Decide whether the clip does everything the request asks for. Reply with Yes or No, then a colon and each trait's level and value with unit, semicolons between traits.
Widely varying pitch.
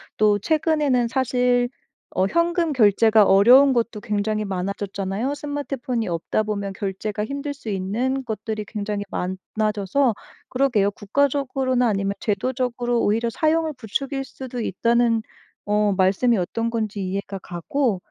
No: average, 4.4 semitones